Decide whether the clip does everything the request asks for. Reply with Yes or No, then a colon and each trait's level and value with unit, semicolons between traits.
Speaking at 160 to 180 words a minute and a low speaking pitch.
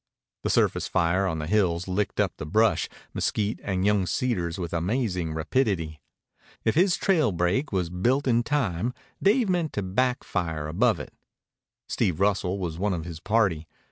Yes: average, 170 wpm; very low, 95 Hz